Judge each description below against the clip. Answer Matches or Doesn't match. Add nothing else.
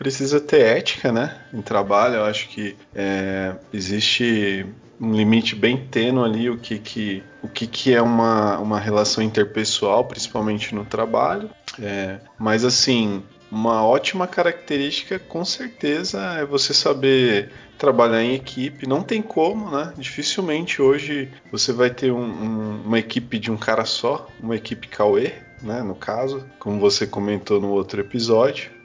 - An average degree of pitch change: Matches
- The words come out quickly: Doesn't match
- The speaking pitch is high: Doesn't match